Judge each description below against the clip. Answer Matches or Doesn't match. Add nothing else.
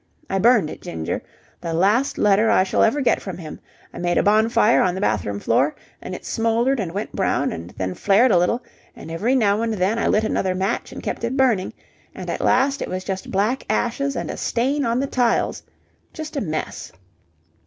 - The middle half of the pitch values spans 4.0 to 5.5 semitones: Matches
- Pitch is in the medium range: Doesn't match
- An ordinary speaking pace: Doesn't match